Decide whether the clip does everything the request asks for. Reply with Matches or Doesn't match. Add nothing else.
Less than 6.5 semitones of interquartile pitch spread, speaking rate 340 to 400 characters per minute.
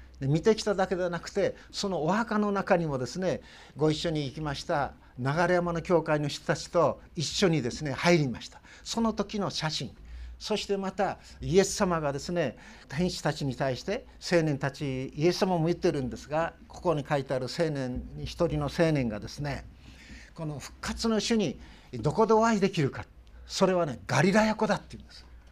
Matches